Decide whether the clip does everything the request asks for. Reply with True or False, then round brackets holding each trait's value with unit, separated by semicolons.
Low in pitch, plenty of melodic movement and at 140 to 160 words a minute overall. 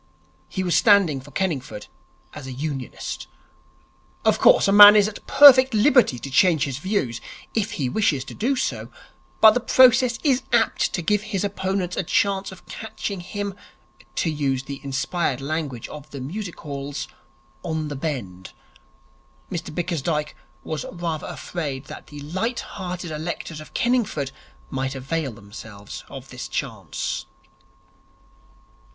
False (165 Hz; 6.7 semitones; 145 wpm)